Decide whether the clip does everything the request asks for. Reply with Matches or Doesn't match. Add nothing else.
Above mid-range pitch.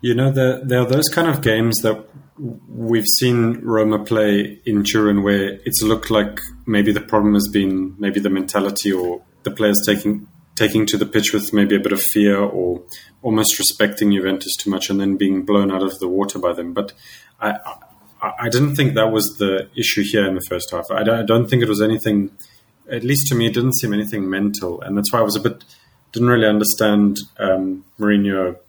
Doesn't match